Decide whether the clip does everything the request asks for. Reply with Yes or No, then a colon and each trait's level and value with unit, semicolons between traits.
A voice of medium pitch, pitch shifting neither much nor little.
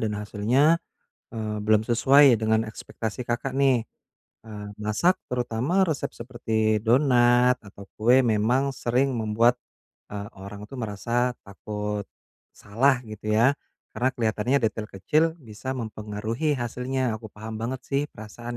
No: low, 115 Hz; average, 3.3 semitones